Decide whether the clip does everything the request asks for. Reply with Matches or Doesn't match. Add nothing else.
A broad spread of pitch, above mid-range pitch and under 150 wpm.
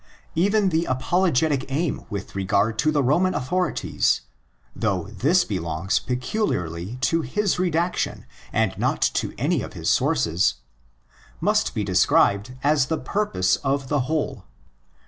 Doesn't match